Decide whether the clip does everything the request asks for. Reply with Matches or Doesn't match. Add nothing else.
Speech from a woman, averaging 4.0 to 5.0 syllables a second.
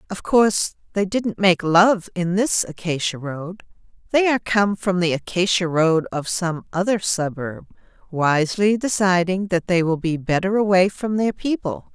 Matches